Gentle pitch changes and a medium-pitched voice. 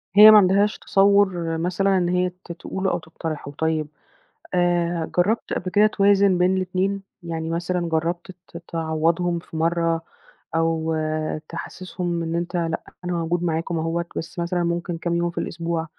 Yes: narrow, 1.8 semitones; medium, 170 Hz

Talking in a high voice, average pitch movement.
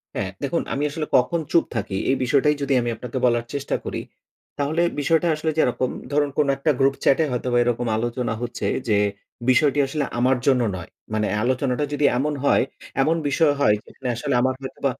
No: low, 135 Hz; average, 3.2 semitones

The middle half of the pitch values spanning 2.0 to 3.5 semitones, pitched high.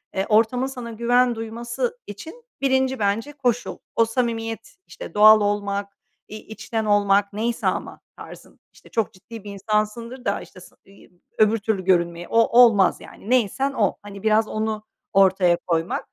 Yes: average, 2.8 semitones; high, 220 Hz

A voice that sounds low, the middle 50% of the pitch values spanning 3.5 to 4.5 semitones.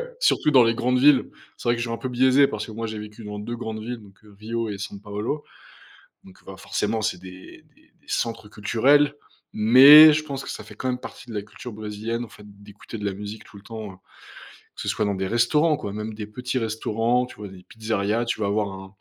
No: low, 110 Hz; average, 2.8 semitones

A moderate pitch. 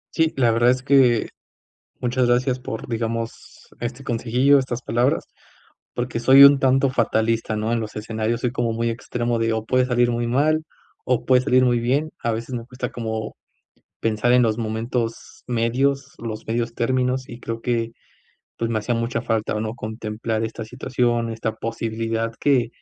No: low, 120 Hz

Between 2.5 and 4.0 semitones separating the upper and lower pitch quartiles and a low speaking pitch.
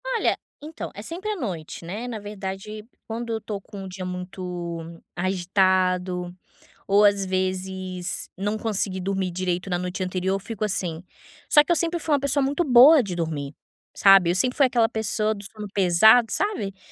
No: average, 3.6 semitones; high, 195 Hz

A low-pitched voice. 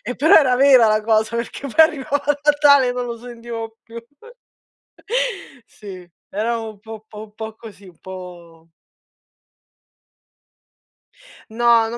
No: high, 225 Hz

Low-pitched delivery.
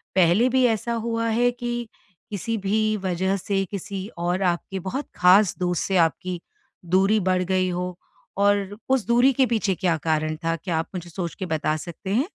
No: high, 190 Hz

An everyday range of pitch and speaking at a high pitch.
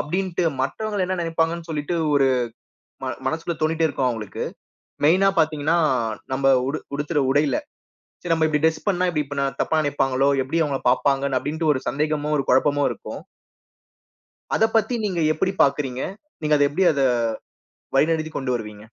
No: average, 3.1 semitones; medium, 150 Hz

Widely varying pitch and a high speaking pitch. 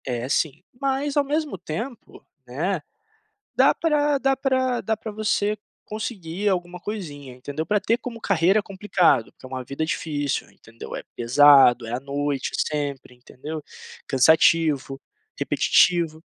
No: wide, 7.5 semitones; medium, 165 Hz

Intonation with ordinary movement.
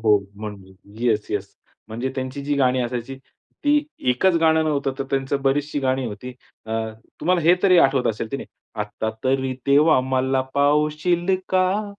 Yes: average, 3.8 semitones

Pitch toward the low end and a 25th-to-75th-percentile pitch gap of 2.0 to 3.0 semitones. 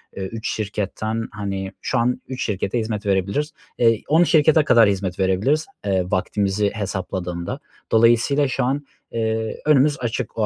No: low, 110 Hz; average, 4.5 semitones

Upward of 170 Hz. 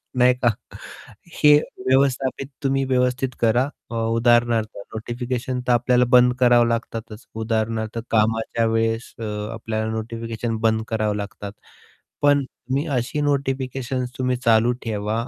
No: low, 120 Hz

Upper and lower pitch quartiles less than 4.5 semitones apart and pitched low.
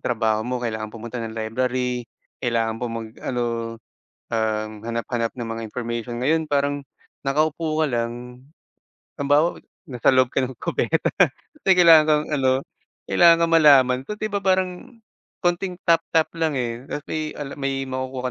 No: average, 4.8 semitones; low, 130 Hz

